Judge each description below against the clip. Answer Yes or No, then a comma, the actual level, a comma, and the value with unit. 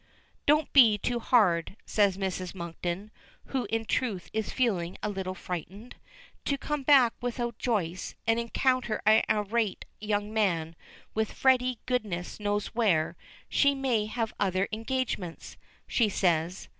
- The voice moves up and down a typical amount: Yes, average, 4.5 semitones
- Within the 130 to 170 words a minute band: Yes, slow, 135 wpm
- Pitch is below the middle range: No, high, 215 Hz